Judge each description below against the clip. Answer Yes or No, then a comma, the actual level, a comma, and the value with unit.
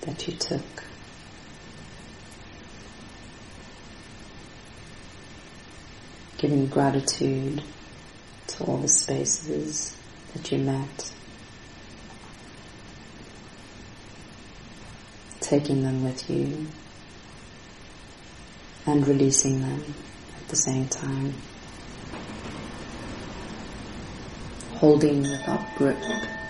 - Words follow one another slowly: Yes, slow, 60 wpm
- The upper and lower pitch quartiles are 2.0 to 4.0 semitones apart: No, average, 4.9 semitones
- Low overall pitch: Yes, low, 130 Hz